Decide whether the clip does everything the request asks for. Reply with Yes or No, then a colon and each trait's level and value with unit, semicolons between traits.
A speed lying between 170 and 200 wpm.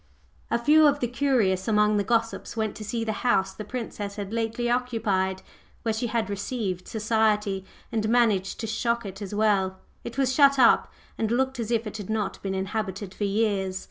Yes: average, 195 wpm